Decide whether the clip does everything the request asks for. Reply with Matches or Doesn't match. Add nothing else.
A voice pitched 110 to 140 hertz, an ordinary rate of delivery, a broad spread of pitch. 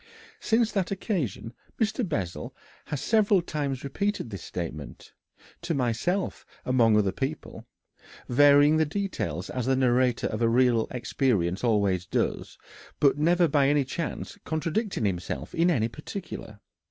Doesn't match